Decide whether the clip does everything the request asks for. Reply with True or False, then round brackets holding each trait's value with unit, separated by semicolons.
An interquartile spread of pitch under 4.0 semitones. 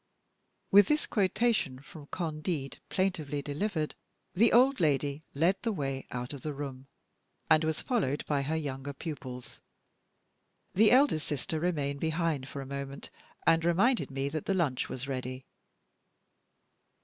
False (4.6 semitones)